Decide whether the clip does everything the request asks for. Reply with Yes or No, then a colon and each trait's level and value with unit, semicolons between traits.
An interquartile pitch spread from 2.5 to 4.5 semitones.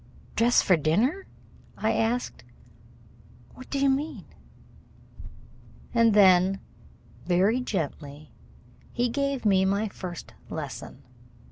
No: average, 5.2 semitones